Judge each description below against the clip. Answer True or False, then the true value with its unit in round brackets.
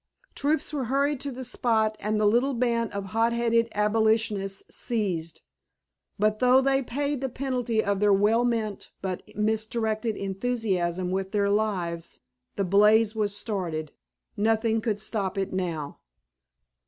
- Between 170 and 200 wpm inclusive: False (140 wpm)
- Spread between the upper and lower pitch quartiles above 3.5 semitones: False (3.1 semitones)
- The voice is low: False (215 Hz)